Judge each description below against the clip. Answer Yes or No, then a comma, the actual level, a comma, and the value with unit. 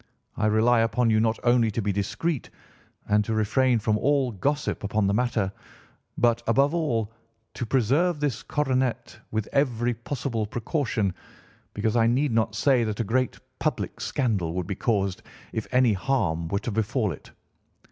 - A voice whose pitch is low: Yes, low, 115 Hz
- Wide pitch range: No, average, 3.3 semitones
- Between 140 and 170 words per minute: Yes, average, 165 wpm